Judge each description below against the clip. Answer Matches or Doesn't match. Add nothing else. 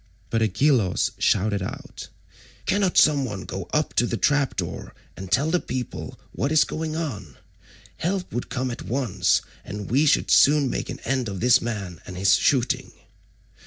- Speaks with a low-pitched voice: Matches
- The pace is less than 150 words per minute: Doesn't match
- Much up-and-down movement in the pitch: Matches